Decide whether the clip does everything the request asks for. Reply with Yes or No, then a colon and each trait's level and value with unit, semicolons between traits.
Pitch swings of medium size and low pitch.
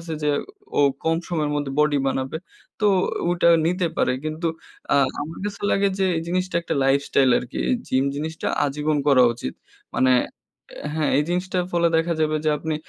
No: average, 3.2 semitones; medium, 155 Hz